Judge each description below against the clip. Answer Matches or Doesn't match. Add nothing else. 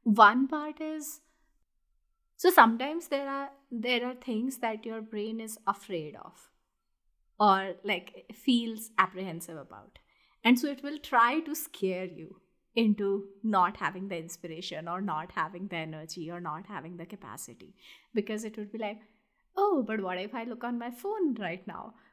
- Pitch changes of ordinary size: Doesn't match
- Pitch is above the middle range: Matches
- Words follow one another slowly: Doesn't match